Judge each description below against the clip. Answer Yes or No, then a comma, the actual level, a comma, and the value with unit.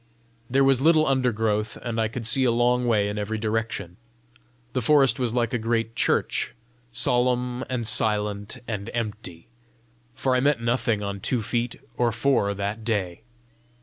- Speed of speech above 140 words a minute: Yes, average, 160 wpm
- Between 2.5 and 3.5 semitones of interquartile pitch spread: Yes, average, 2.8 semitones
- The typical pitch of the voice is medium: No, low, 115 Hz